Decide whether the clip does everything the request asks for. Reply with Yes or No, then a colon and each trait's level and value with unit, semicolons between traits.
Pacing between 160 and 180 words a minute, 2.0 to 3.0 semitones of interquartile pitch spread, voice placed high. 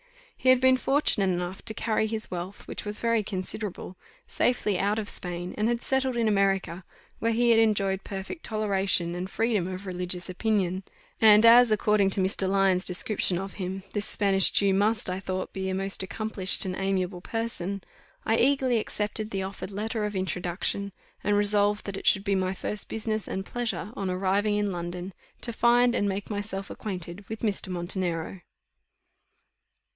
Yes: average, 175 wpm; narrow, 2.6 semitones; high, 200 Hz